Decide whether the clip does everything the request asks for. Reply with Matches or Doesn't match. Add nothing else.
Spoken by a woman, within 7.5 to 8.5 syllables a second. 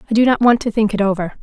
Matches